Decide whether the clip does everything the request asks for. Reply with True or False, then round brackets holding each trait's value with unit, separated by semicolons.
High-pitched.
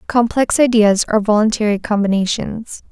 True (215 Hz)